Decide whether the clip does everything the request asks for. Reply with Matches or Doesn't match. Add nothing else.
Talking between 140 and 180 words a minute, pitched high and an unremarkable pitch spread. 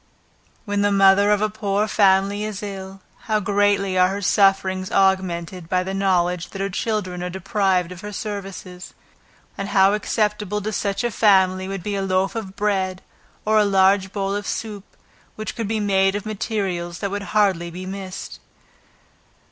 Doesn't match